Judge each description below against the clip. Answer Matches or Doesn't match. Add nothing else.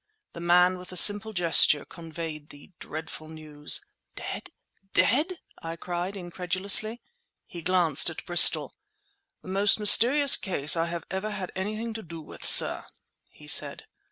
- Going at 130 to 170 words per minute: Matches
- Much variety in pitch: Doesn't match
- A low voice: Doesn't match